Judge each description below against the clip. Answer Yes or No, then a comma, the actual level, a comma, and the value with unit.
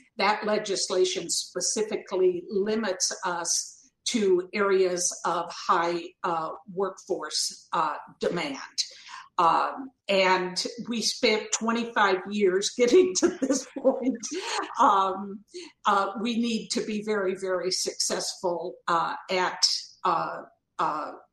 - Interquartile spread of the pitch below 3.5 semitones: No, average, 4.2 semitones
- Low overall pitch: No, high, 205 Hz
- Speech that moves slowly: Yes, slow, 100 wpm